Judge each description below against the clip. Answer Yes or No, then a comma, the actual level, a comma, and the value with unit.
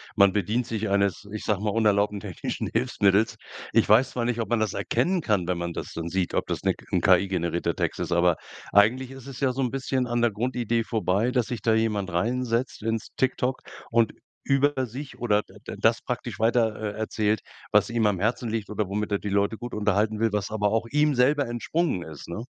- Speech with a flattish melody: No, average, 3.2 semitones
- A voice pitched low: Yes, low, 110 Hz